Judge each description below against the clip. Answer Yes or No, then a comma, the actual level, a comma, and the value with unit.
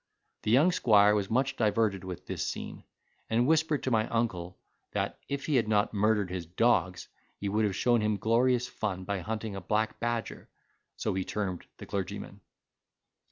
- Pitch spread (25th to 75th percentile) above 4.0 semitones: No, average, 3.3 semitones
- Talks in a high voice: No, low, 110 Hz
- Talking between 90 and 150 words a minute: No, average, 175 wpm